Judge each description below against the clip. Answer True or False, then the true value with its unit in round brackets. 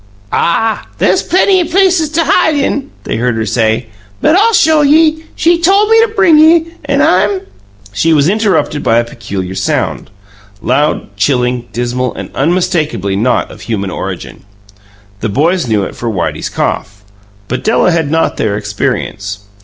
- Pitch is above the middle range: False (155 Hz)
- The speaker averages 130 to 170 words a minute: True (160 wpm)